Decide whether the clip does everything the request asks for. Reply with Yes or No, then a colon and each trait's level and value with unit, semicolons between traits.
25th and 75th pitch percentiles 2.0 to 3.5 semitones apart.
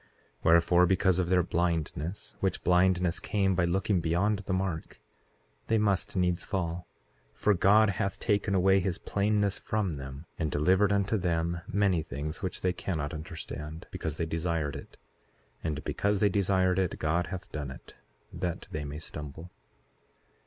Yes: average, 3.0 semitones